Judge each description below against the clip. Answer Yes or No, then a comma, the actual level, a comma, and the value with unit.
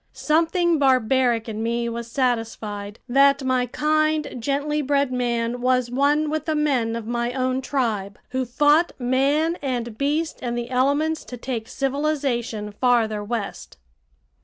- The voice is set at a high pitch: Yes, very high, 255 Hz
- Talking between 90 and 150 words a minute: Yes, average, 140 wpm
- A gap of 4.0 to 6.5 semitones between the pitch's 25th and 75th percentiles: No, average, 3.6 semitones